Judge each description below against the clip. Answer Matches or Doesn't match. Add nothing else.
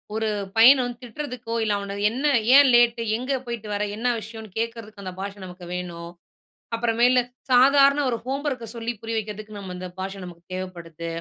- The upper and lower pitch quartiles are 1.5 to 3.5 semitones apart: Doesn't match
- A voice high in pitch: Matches